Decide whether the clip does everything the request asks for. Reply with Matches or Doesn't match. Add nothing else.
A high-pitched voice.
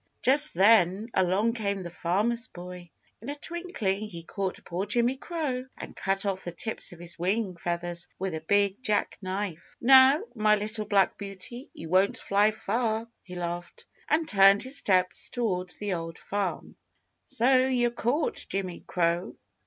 Matches